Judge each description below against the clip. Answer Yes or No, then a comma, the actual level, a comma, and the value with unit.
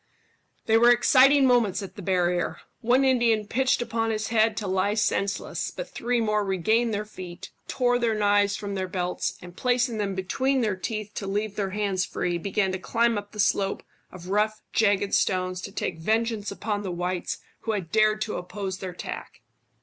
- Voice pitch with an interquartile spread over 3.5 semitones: No, average, 3.0 semitones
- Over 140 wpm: Yes, average, 190 wpm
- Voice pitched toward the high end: Yes, high, 210 Hz